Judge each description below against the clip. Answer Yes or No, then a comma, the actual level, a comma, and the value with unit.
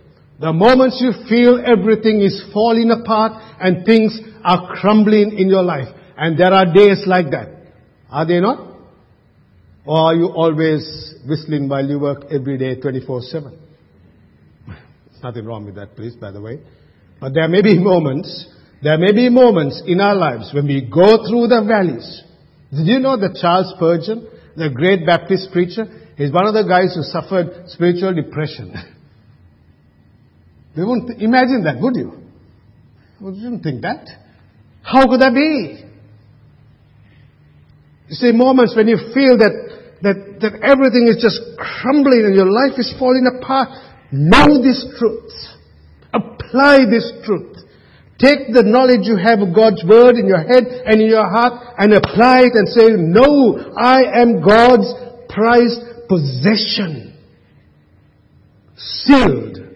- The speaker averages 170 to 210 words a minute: No, average, 150 wpm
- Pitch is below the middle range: No, high, 190 Hz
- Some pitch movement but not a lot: No, wide, 8.0 semitones